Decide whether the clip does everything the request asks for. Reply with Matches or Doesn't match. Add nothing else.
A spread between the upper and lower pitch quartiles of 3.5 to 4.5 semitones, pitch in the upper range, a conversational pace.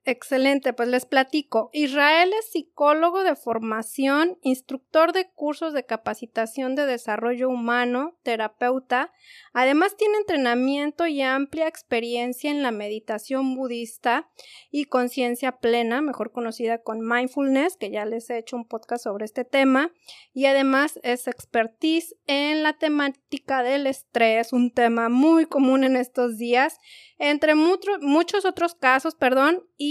Matches